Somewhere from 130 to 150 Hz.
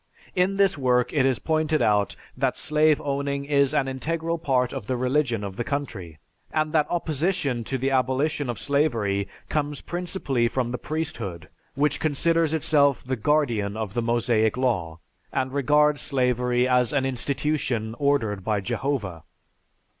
Yes: low, 135 Hz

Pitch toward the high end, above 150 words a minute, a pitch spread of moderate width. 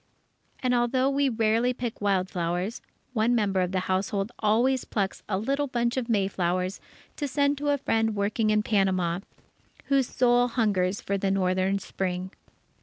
Yes: high, 215 Hz; average, 160 wpm; average, 4.3 semitones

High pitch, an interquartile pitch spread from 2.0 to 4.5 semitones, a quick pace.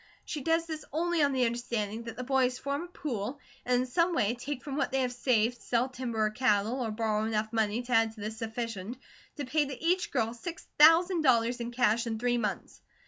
Yes: high, 245 Hz; average, 3.8 semitones; fast, 225 wpm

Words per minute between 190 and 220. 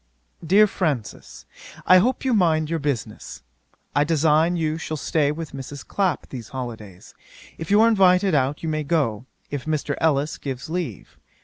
No: average, 165 wpm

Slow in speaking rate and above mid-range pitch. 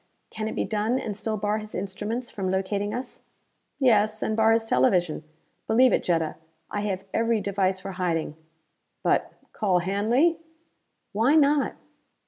No: average, 150 wpm; high, 210 Hz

